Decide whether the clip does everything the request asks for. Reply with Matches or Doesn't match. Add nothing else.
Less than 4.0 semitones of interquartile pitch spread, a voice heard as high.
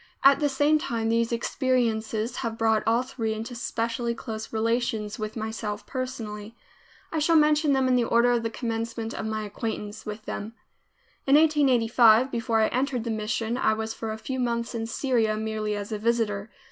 Matches